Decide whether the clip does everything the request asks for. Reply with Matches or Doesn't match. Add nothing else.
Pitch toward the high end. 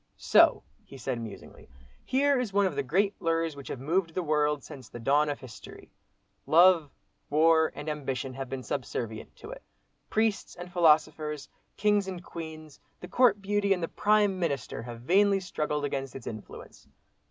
Doesn't match